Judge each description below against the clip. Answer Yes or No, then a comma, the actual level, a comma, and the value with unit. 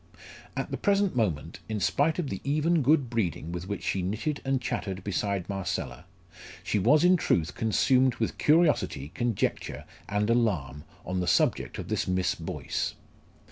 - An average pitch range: No, wide, 7.4 semitones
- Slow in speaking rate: No, average, 160 wpm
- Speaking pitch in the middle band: No, low, 110 Hz